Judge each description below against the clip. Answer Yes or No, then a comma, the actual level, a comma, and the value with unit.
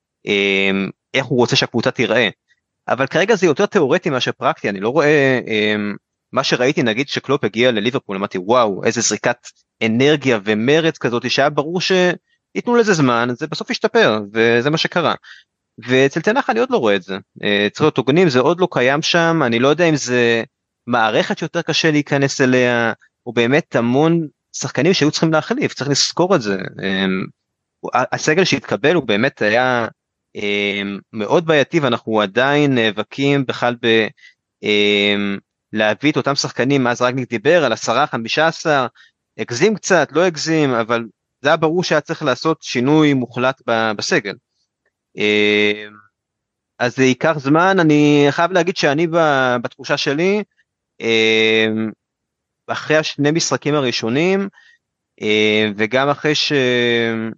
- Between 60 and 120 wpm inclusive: No, average, 130 wpm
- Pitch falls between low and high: No, low, 130 Hz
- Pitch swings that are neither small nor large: No, wide, 5.8 semitones